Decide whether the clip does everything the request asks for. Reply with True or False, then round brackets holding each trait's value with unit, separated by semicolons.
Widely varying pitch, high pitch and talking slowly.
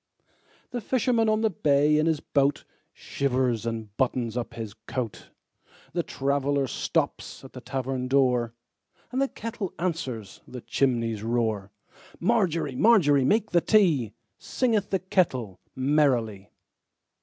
False (7.1 semitones; 135 Hz; 110 wpm)